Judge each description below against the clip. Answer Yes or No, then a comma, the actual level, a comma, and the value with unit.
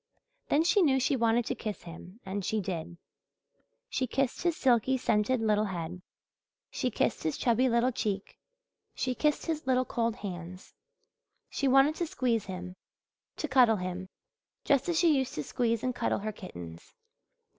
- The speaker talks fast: No, average, 165 wpm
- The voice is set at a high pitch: Yes, high, 230 Hz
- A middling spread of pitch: No, wide, 5.7 semitones